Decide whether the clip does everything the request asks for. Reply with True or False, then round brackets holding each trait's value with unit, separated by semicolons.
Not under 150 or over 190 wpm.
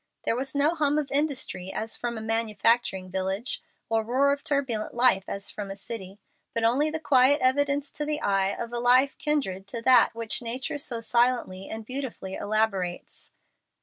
True (180 wpm)